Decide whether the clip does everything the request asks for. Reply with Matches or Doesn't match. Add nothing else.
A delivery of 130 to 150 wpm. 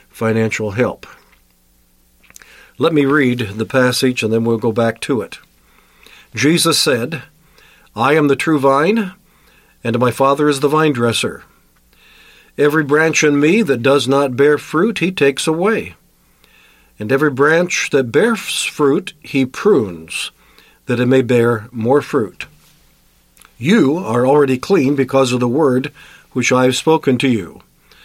Matches